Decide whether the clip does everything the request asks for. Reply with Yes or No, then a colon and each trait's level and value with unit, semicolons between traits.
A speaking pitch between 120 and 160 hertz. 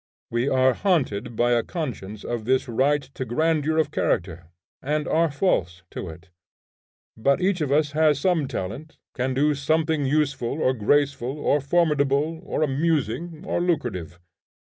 Yes: medium, 140 Hz